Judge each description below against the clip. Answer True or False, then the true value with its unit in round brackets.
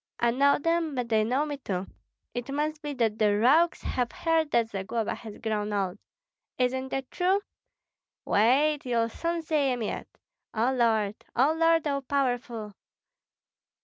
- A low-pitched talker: False (250 Hz)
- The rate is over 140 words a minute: True (150 wpm)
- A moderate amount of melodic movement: True (5.0 semitones)